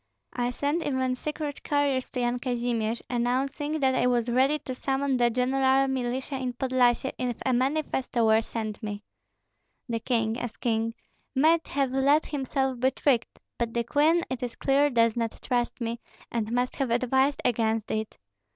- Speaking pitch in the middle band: No, very high, 250 Hz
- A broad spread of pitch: No, narrow, 2.4 semitones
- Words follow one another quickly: No, average, 170 wpm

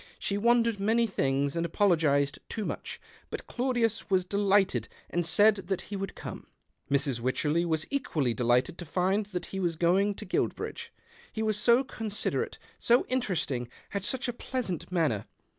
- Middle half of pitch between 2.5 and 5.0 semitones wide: No, wide, 5.6 semitones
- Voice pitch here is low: No, high, 190 Hz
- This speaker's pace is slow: No, average, 160 wpm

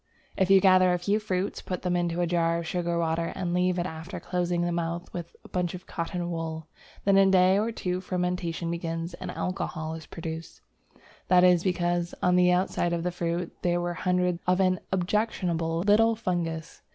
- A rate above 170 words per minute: Yes, average, 200 wpm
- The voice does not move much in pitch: Yes, narrow, 1.4 semitones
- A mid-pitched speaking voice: Yes, medium, 175 Hz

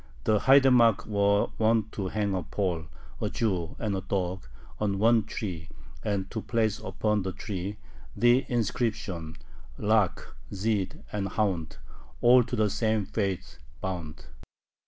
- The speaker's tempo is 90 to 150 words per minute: Yes, slow, 135 wpm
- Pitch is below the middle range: Yes, low, 105 Hz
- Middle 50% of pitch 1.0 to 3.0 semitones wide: Yes, average, 2.7 semitones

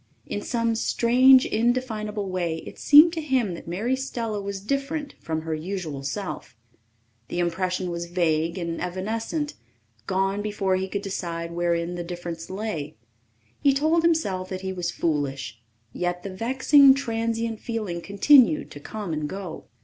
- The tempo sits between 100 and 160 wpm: Yes, average, 150 wpm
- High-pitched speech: Yes, high, 195 Hz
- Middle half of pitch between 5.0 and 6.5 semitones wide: Yes, average, 5.3 semitones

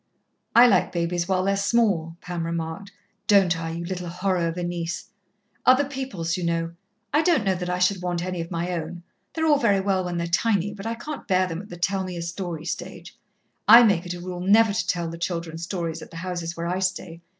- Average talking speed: No, fast, 230 wpm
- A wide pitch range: No, average, 2.8 semitones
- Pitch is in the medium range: Yes, medium, 180 Hz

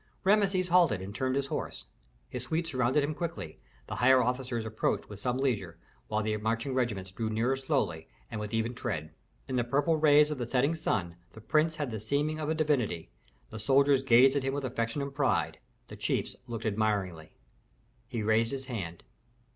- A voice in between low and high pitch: No, low, 125 Hz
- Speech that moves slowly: No, average, 190 wpm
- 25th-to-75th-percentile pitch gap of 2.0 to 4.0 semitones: No, average, 4.6 semitones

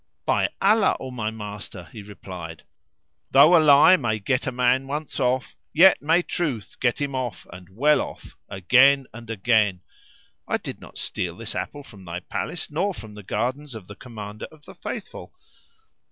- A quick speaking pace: No, average, 175 wpm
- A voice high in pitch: No, low, 125 Hz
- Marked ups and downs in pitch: Yes, wide, 5.7 semitones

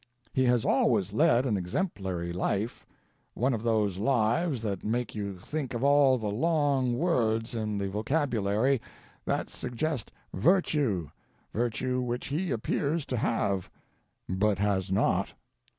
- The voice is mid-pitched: No, low, 120 Hz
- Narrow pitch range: No, average, 5.2 semitones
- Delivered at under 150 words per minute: Yes, slow, 135 wpm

